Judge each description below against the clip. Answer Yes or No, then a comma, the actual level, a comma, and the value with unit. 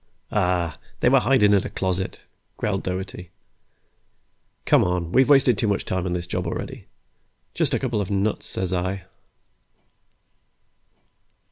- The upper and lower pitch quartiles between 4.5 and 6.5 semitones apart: No, average, 3.6 semitones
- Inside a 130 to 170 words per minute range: Yes, average, 140 wpm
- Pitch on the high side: No, very low, 95 Hz